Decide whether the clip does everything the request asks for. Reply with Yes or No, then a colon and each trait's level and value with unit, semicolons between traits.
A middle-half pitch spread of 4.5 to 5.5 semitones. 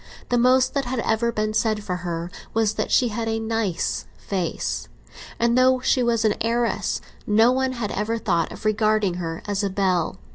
No: average, 2.8 semitones